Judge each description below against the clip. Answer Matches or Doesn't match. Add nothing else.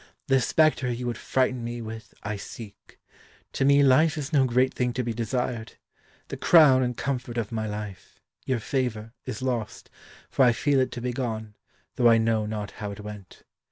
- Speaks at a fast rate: Doesn't match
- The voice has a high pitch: Doesn't match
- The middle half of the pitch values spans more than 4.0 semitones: Doesn't match